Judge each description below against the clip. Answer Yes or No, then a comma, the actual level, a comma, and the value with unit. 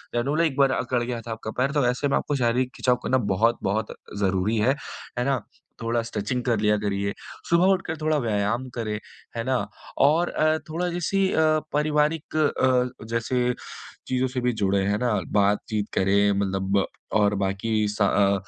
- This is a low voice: Yes, low, 120 Hz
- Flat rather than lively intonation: No, average, 4.7 semitones